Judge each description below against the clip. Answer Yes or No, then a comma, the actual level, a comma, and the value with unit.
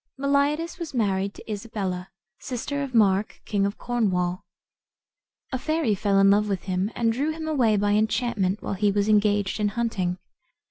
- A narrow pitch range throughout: No, average, 3.8 semitones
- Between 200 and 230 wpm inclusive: No, average, 170 wpm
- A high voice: Yes, high, 210 Hz